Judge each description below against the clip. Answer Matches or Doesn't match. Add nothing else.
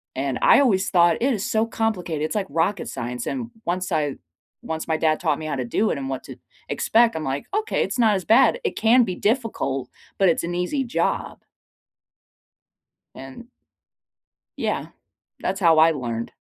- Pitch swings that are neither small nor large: Doesn't match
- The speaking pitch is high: Doesn't match